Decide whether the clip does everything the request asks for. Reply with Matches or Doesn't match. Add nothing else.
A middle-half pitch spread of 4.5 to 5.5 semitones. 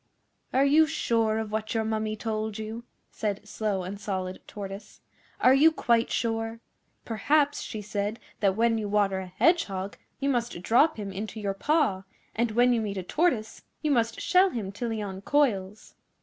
Doesn't match